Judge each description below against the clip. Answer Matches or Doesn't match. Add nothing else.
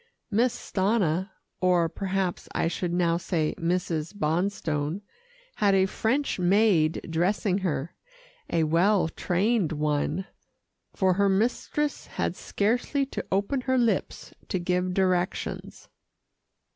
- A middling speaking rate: Doesn't match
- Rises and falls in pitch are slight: Doesn't match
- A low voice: Doesn't match